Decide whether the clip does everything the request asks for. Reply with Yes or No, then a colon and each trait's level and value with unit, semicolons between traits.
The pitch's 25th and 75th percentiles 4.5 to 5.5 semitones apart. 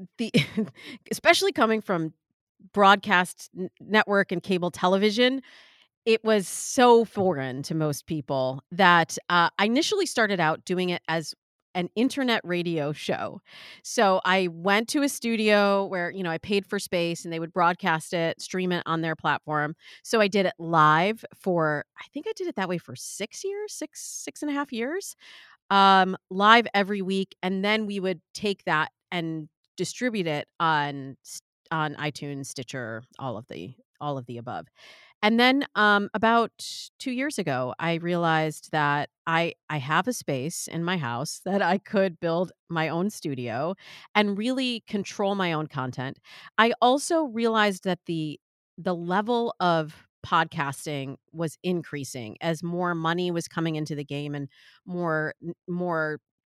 Yes: average, 5.0 semitones